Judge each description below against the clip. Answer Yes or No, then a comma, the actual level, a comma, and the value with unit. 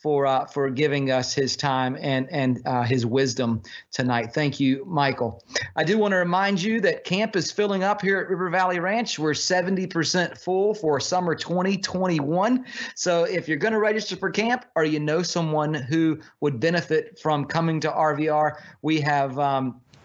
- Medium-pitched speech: Yes, medium, 155 Hz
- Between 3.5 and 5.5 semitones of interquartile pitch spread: Yes, average, 4.9 semitones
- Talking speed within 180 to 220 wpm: Yes, average, 190 wpm